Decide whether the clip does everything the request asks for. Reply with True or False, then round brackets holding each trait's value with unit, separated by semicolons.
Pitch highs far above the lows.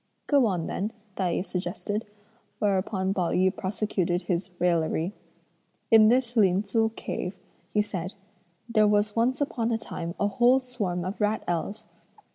False (3.6 semitones)